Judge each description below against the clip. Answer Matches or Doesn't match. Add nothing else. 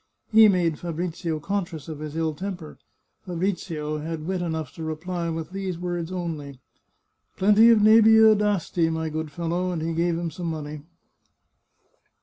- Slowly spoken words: Doesn't match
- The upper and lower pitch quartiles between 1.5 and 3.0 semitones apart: Matches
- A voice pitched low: Doesn't match